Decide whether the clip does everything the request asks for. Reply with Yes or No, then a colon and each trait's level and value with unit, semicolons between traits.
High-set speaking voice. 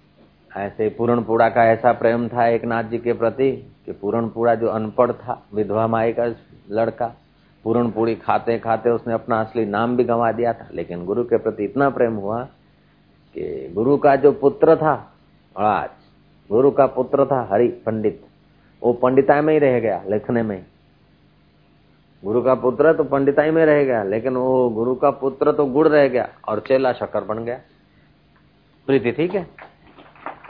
No: low, 120 Hz